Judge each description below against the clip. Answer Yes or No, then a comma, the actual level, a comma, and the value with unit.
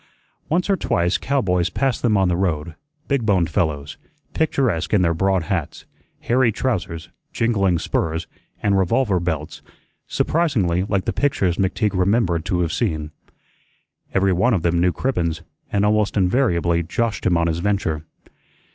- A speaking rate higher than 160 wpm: No, average, 145 wpm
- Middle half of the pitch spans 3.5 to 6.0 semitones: Yes, average, 4.2 semitones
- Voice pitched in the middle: No, very low, 95 Hz